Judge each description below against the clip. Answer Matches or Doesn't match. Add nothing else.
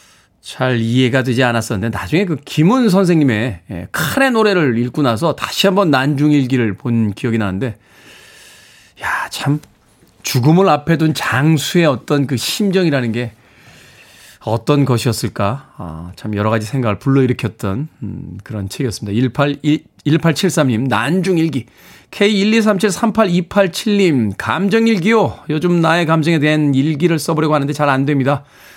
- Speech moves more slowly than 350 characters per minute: Matches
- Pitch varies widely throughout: Matches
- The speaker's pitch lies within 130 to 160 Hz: Matches